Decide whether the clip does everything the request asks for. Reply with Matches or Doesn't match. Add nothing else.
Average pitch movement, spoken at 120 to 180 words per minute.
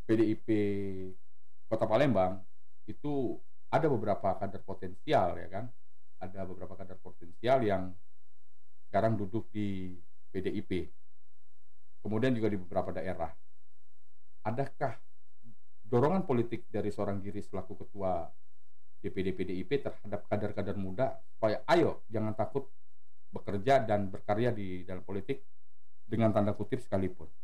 Doesn't match